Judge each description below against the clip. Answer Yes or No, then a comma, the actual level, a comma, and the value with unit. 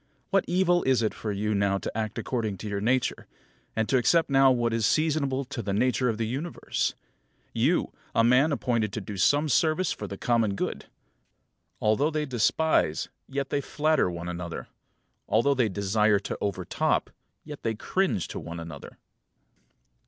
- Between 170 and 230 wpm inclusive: Yes, average, 175 wpm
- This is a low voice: Yes, low, 115 Hz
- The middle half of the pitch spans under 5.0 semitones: No, wide, 5.4 semitones